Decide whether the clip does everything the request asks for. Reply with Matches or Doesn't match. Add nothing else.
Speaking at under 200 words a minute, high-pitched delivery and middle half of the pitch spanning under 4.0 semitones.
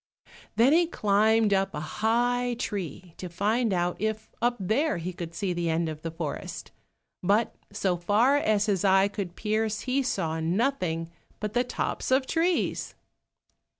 Doesn't match